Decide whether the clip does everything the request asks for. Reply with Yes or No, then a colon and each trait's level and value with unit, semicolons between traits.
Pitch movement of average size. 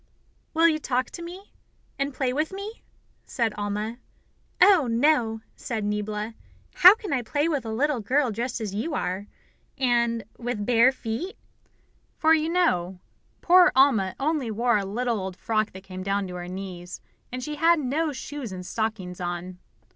No: wide, 6.3 semitones